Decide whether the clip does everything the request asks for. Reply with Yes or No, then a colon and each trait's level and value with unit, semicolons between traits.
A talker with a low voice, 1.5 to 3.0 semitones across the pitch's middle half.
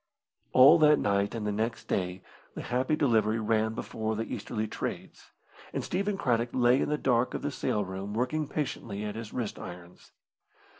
No: low, 115 Hz; average, 3.7 semitones